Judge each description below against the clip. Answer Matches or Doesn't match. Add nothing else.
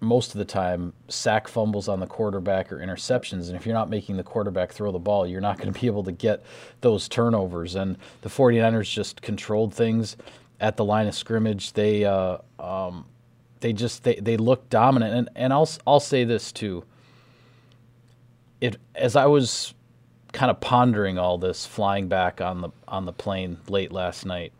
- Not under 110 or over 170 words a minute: Doesn't match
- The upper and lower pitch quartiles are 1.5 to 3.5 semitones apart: Doesn't match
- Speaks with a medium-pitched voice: Doesn't match